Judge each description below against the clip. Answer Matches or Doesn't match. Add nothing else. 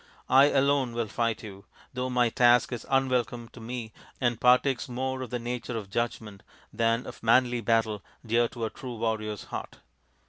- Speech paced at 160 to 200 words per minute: Matches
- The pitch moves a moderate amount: Doesn't match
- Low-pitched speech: Matches